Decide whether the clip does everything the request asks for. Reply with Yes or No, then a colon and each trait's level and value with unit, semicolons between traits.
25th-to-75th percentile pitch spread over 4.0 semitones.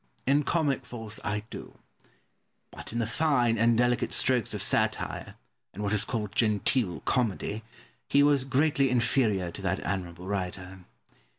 Yes: average, 4.6 semitones